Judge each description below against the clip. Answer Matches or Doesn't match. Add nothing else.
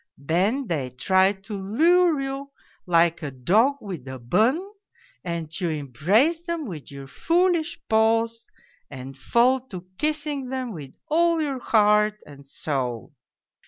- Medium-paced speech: Doesn't match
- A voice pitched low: Doesn't match